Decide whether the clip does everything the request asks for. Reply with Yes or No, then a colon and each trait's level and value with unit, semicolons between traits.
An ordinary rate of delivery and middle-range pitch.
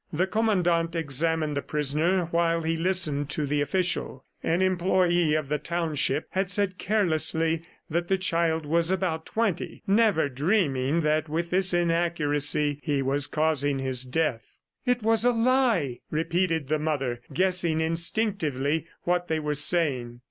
Yes: average, 145 wpm; medium, 165 Hz